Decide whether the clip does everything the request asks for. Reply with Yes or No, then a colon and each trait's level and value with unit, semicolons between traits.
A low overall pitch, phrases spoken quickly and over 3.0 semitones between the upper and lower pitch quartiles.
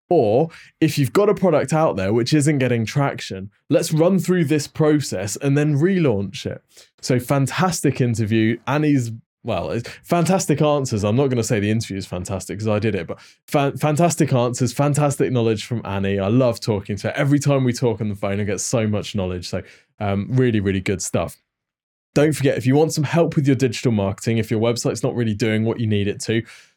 Yes: low, 125 Hz; fast, 210 wpm; wide, 5.4 semitones